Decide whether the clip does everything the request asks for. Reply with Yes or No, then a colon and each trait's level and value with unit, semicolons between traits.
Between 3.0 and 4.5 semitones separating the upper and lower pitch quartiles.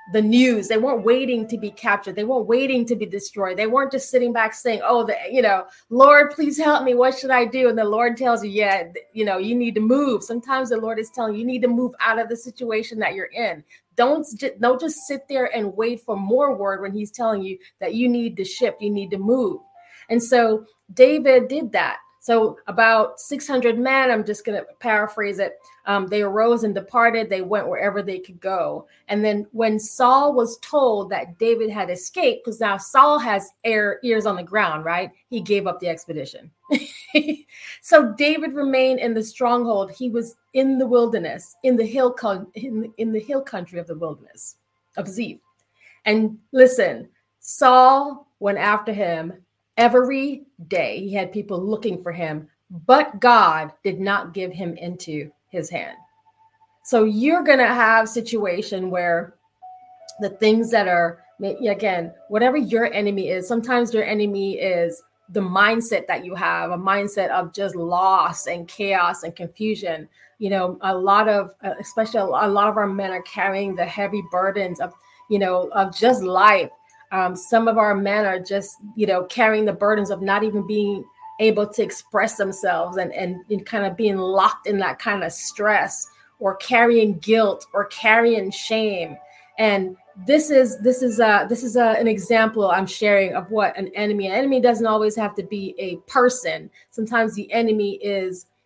Yes: average, 3.9 semitones